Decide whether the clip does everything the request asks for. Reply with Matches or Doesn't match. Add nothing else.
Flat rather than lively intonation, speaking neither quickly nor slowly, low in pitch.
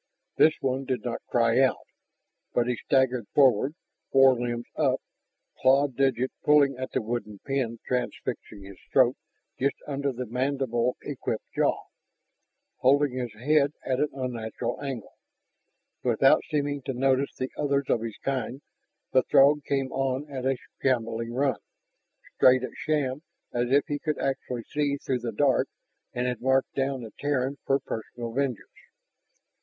Matches